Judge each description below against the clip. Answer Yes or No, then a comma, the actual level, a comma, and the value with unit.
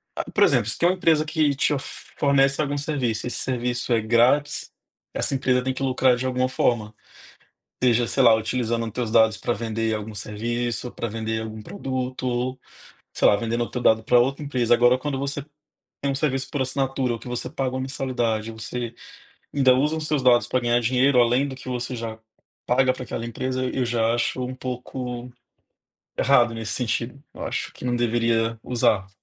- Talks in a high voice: No, low, 125 Hz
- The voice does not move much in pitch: Yes, narrow, 2.3 semitones